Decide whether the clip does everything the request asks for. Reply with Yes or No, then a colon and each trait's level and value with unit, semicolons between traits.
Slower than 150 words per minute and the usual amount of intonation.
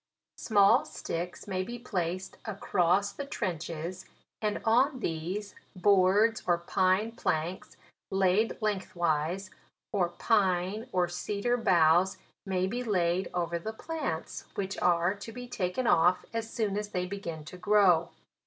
Yes: slow, 135 wpm; average, 3.3 semitones